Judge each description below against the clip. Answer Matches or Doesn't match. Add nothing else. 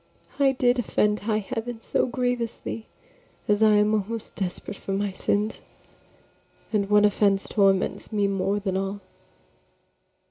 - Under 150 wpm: Matches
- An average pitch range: Doesn't match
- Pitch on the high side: Matches